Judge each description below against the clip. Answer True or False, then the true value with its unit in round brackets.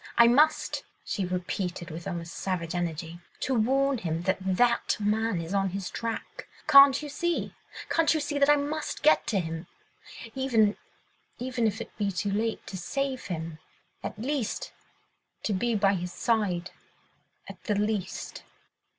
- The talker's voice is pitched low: False (210 Hz)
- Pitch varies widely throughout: True (6.2 semitones)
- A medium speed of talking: True (155 wpm)